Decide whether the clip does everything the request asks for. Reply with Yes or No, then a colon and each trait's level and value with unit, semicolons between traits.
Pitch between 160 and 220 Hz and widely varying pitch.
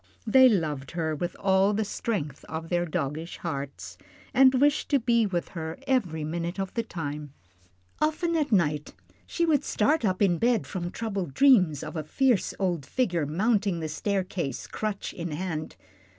Yes: medium, 185 Hz; wide, 6.3 semitones